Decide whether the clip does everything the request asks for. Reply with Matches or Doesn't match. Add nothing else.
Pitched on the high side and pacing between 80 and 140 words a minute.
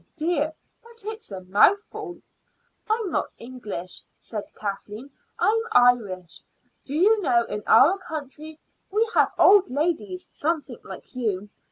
Matches